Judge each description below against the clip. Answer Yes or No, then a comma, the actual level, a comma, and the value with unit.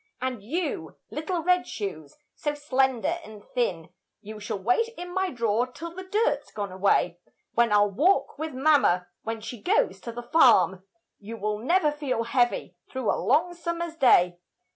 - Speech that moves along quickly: No, average, 165 wpm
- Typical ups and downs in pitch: No, wide, 7.6 semitones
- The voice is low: No, high, 245 Hz